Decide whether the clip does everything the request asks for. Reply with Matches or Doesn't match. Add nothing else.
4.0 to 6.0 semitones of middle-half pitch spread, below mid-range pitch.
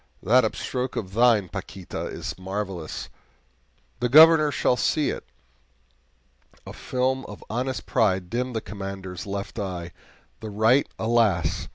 Matches